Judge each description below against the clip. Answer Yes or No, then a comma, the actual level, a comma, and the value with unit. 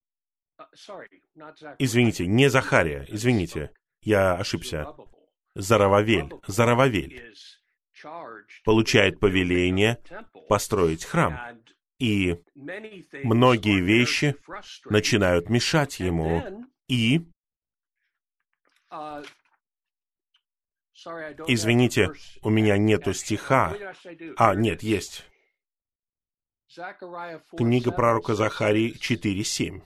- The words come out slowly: Yes, slow, 60 wpm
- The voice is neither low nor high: No, low, 115 Hz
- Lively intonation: No, average, 5.0 semitones